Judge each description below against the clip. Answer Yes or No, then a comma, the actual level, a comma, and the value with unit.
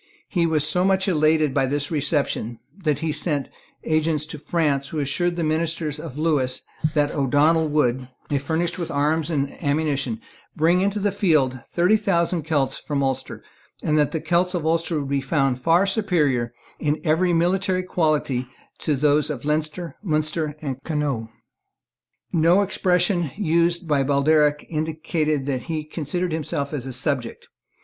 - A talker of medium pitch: Yes, medium, 155 Hz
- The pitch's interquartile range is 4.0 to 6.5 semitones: No, average, 3.0 semitones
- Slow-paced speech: No, average, 160 wpm